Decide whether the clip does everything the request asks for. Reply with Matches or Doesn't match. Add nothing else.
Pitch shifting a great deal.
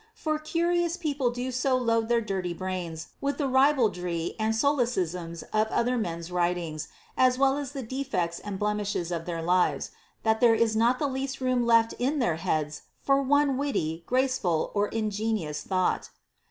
Matches